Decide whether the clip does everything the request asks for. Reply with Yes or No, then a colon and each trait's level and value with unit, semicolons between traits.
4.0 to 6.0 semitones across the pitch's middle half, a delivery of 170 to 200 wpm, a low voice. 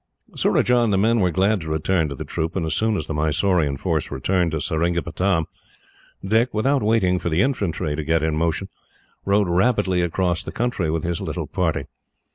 Yes: average, 4.5 semitones; average, 195 wpm; very low, 90 Hz